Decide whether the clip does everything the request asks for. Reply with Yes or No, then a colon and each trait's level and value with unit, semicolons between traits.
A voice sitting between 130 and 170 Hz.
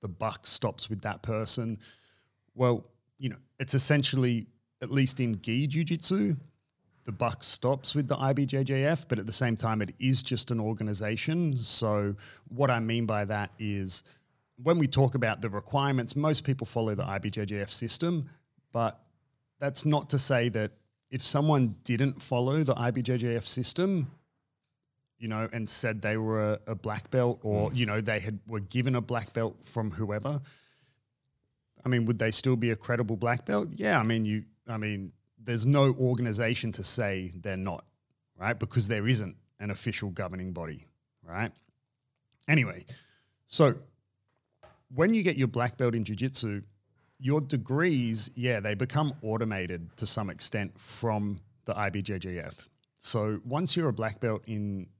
No: low, 120 Hz